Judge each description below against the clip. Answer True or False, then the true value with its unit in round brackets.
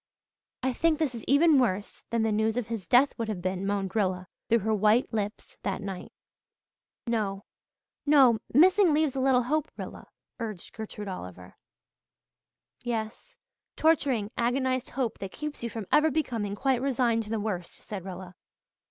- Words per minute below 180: True (160 wpm)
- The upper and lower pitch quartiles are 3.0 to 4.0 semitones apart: False (4.7 semitones)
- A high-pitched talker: True (230 Hz)